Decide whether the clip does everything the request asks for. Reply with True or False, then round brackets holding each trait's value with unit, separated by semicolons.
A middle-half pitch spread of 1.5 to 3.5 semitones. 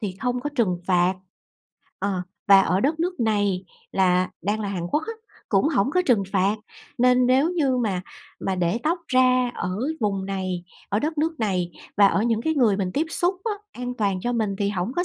False (5.1 semitones)